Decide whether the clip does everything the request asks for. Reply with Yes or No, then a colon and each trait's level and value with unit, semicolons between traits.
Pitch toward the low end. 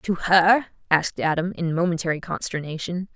No: medium, 175 Hz